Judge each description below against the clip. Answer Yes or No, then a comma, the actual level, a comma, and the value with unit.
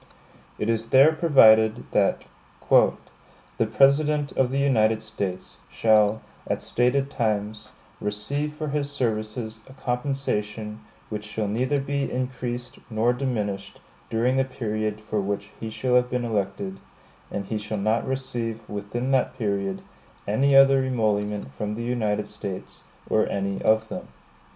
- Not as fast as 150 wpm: Yes, average, 140 wpm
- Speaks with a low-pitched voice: Yes, low, 110 Hz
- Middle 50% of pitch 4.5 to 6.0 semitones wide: No, average, 3.9 semitones